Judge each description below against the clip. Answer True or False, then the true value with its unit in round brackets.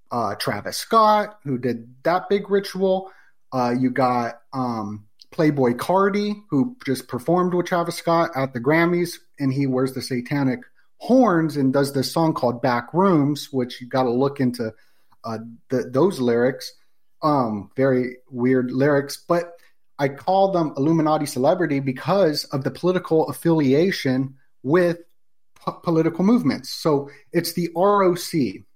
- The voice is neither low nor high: True (145 Hz)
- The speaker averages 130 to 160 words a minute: True (145 wpm)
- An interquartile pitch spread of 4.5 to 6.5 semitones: True (5.1 semitones)